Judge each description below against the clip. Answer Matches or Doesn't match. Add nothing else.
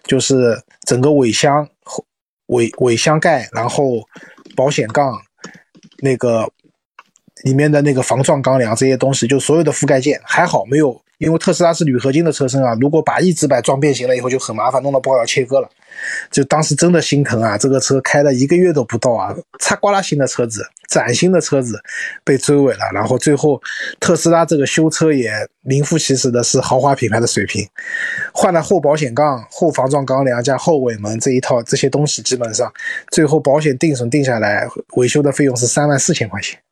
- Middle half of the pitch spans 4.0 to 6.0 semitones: Doesn't match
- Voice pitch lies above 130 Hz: Matches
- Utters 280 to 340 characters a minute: Matches